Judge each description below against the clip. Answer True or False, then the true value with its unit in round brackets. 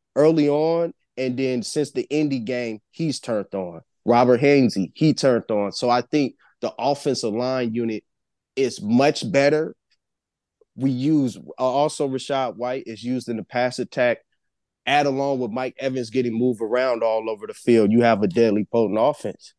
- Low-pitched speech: True (130 Hz)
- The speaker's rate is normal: True (170 wpm)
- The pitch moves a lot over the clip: False (3.2 semitones)